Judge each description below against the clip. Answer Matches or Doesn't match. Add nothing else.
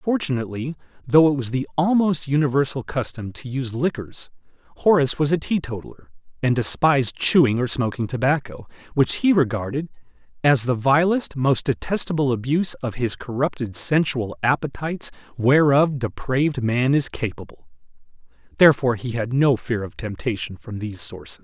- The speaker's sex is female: Doesn't match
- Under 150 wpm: Matches